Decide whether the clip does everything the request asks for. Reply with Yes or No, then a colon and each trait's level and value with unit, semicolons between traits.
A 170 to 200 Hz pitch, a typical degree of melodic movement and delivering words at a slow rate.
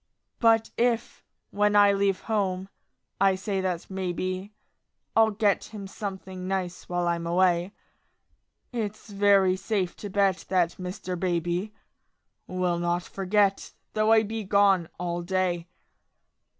No: high, 190 Hz; narrow, 2.3 semitones; slow, 125 wpm